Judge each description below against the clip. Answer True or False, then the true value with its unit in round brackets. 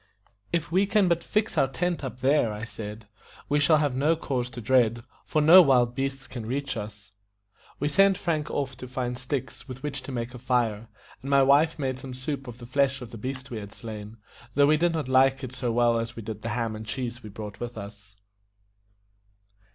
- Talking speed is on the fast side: True (220 wpm)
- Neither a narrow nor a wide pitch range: True (3.6 semitones)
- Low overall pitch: True (130 Hz)